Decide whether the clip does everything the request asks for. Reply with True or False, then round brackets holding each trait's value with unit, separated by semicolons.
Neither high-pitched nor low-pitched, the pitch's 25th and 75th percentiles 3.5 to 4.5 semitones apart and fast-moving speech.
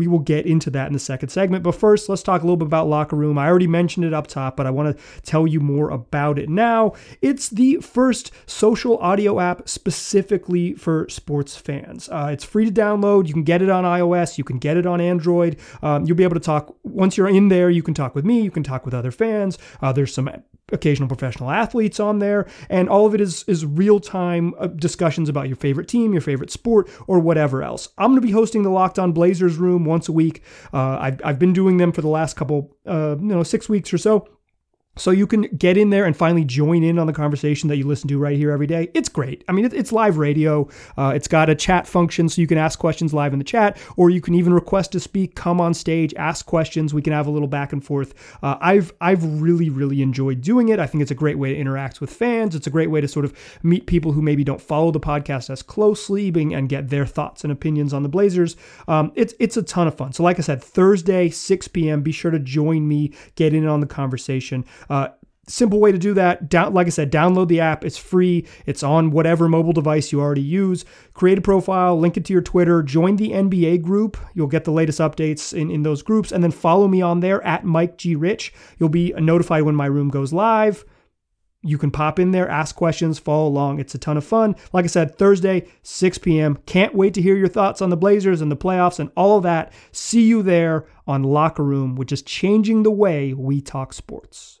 True (165 Hz; 4.2 semitones; 245 wpm)